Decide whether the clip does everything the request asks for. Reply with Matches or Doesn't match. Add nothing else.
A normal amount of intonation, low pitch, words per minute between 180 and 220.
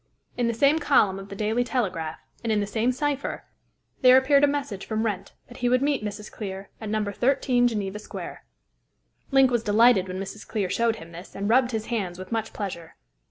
Doesn't match